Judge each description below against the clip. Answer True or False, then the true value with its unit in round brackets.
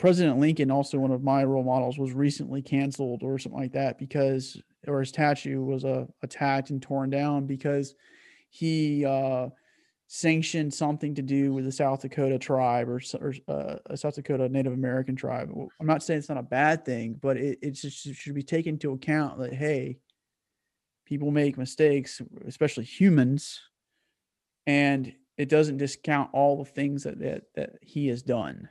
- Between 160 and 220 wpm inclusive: True (175 wpm)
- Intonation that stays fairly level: True (1.8 semitones)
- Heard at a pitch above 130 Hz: True (140 Hz)